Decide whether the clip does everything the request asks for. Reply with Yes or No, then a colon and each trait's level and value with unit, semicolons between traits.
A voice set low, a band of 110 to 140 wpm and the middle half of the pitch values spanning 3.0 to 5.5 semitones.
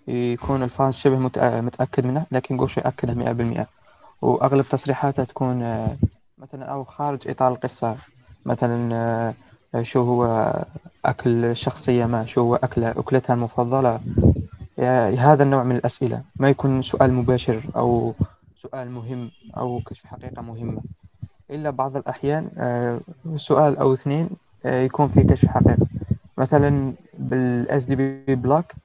No: low, 125 Hz; average, 120 wpm; narrow, 2.4 semitones